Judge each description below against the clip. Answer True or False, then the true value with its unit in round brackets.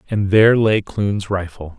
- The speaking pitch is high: False (100 Hz)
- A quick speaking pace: False (170 wpm)